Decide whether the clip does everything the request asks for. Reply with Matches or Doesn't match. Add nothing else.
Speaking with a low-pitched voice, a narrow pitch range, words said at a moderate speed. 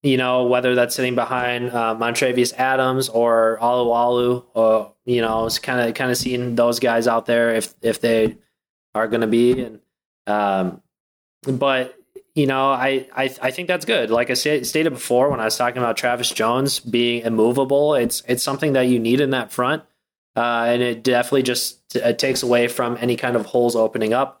Matches